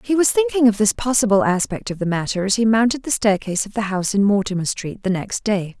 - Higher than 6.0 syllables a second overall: Yes, 6.2 syllables/s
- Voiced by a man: No, female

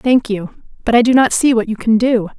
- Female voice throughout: Yes, female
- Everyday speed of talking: No, fast, 275 wpm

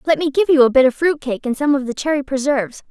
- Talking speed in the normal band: No, fast, 310 wpm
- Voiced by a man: No, female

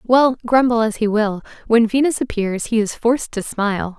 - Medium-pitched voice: No, high, 225 Hz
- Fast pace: No, average, 195 wpm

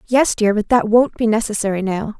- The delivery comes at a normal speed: No, fast, 220 wpm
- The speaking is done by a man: No, female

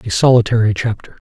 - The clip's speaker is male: Yes, male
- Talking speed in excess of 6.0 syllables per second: Yes, 6.4 syllables/s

